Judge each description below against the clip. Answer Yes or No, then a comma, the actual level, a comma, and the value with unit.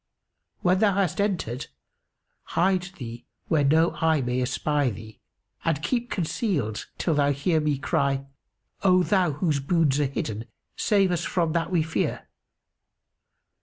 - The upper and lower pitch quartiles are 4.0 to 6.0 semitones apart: Yes, average, 4.8 semitones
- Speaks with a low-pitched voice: No, medium, 160 Hz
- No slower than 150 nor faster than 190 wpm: No, average, 140 wpm